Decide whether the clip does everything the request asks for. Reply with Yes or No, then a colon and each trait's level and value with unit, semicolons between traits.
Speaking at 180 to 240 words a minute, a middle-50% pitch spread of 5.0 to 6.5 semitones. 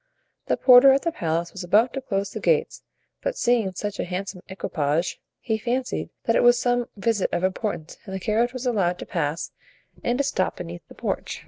Yes: fast, 205 wpm; average, 5.3 semitones